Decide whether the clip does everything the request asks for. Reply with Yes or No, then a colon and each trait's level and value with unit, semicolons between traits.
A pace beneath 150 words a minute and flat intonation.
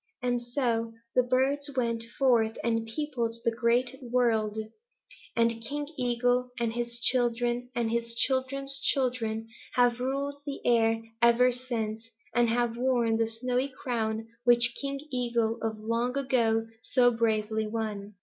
Yes: average, 140 wpm; narrow, 1.8 semitones